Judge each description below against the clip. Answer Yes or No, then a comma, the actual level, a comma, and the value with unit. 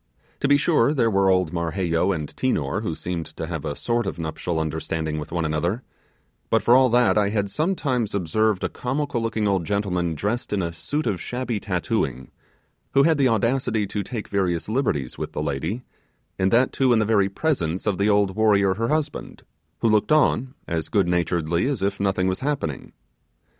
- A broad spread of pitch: Yes, wide, 5.8 semitones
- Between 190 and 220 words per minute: Yes, average, 195 wpm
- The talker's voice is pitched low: Yes, low, 100 Hz